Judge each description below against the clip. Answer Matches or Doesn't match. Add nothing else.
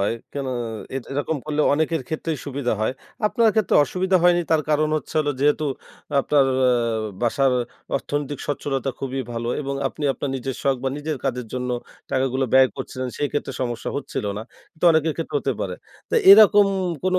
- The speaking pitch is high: Doesn't match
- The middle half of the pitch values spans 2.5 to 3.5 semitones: Matches